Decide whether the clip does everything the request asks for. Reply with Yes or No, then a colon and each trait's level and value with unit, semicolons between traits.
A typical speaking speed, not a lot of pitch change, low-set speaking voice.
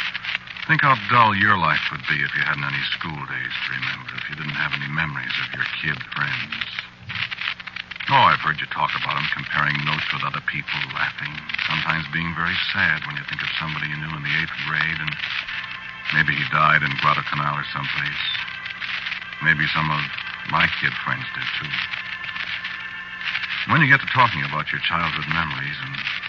Yes: average, 180 wpm; narrow, 1.4 semitones; very low, 75 Hz